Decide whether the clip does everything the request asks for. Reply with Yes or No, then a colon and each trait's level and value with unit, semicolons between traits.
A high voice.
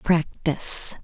No: medium, 160 Hz